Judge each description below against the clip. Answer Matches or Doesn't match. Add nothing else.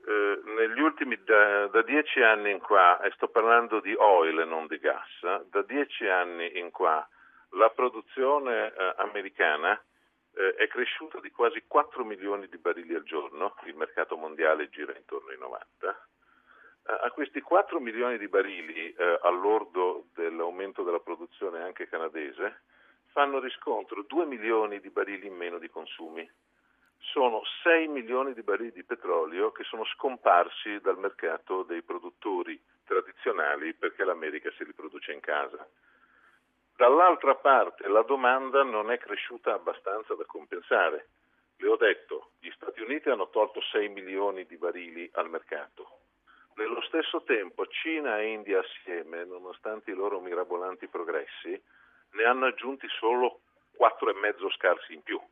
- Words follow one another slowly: Doesn't match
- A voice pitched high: Matches